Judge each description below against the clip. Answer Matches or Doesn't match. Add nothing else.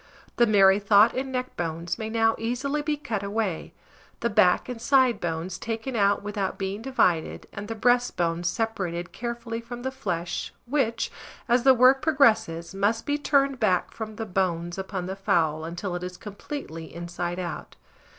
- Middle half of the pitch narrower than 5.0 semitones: Doesn't match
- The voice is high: Matches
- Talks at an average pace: Matches